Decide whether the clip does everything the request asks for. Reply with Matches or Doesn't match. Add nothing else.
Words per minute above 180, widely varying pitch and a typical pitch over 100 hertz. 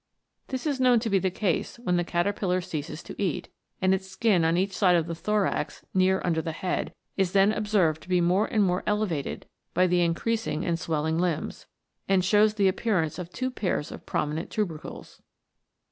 Doesn't match